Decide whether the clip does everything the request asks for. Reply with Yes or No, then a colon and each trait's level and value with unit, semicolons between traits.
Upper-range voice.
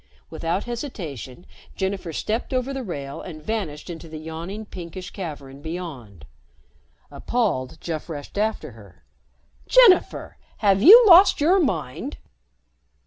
No: medium, 180 Hz